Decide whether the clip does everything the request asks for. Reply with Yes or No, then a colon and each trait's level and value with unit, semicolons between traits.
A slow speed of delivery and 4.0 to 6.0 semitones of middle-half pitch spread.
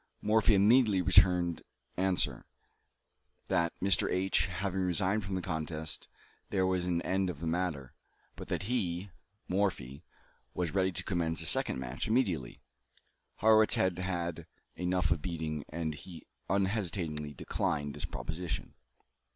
No: slow, 130 wpm; average, 3.0 semitones